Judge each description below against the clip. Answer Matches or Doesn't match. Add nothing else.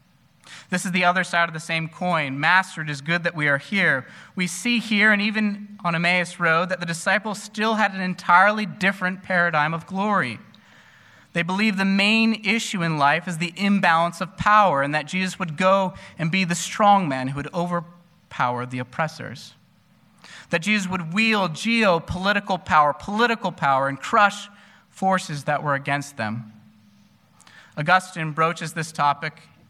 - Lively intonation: Doesn't match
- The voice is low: Doesn't match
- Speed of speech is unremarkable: Matches